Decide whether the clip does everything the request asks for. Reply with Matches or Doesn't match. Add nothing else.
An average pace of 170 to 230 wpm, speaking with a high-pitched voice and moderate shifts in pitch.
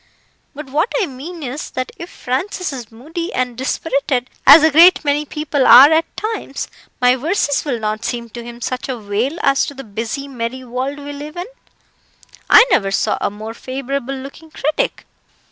Matches